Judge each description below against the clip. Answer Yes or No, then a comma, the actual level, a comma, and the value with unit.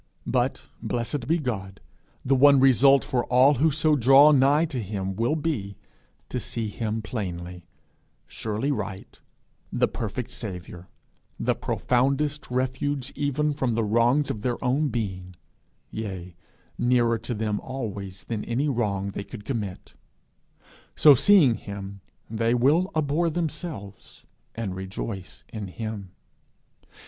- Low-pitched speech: Yes, low, 120 Hz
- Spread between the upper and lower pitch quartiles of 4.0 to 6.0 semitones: Yes, wide, 5.5 semitones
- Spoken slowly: Yes, slow, 130 wpm